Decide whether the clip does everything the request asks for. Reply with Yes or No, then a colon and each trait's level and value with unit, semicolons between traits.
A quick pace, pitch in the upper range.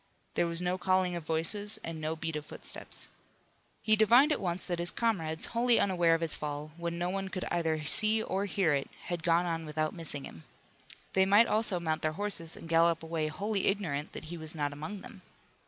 No: fast, 210 wpm; medium, 170 Hz